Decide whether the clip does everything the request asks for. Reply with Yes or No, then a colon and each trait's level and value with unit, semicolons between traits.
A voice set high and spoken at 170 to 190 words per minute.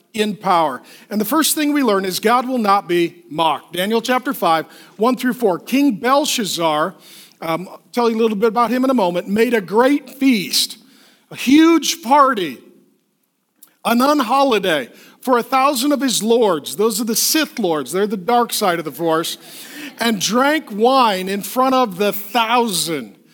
Yes: high, 235 Hz; average, 175 wpm